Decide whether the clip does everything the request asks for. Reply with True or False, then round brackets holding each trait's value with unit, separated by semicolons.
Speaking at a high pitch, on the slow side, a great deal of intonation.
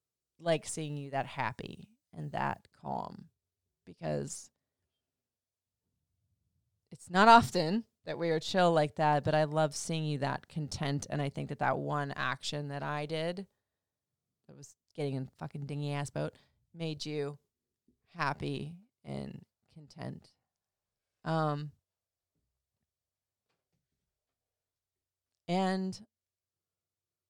False (145 Hz; 110 wpm; 7.8 semitones)